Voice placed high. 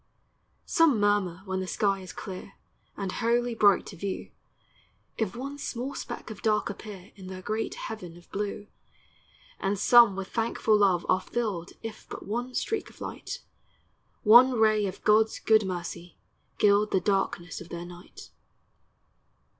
Yes: high, 205 Hz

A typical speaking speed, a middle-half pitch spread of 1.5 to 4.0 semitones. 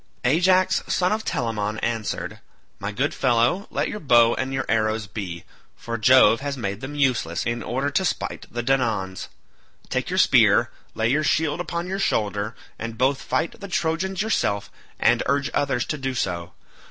No: average, 170 wpm; average, 5.3 semitones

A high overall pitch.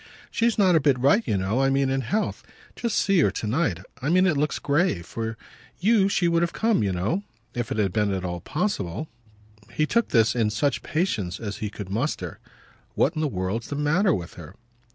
No: low, 135 Hz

